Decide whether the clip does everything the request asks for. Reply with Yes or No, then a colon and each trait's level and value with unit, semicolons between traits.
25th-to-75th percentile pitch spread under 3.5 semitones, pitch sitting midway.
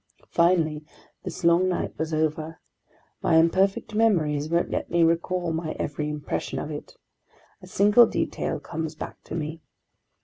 Yes: narrow, 2.5 semitones; medium, 165 Hz